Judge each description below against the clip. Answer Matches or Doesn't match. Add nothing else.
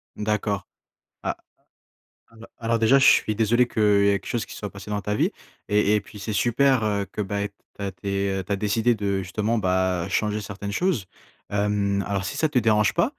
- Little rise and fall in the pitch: Matches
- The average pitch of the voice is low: Matches